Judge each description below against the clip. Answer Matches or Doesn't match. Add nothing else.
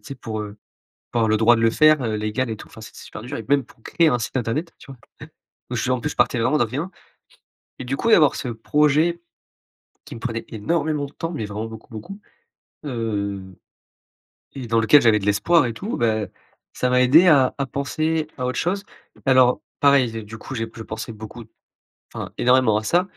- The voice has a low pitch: Matches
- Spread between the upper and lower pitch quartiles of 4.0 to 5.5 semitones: Matches